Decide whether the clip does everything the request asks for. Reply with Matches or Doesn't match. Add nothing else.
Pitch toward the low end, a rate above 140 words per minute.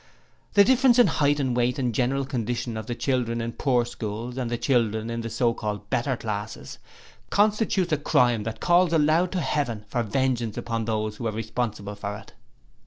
Matches